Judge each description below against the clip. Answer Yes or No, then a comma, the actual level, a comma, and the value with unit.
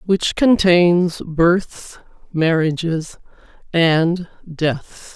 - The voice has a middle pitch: Yes, medium, 170 Hz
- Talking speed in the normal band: No, slow, 70 wpm